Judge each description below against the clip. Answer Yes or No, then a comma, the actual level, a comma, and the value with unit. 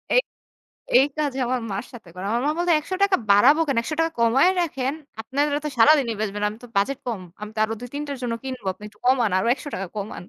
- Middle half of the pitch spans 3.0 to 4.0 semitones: No, average, 5.2 semitones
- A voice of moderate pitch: No, very high, 255 Hz